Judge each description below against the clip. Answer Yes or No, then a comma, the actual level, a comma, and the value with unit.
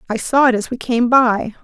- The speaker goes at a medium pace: No, fast, 255 wpm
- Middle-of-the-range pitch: No, high, 240 Hz